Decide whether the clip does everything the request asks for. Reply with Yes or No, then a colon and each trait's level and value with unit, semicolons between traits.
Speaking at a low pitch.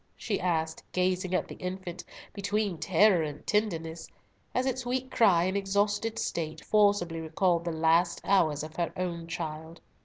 No: medium, 180 Hz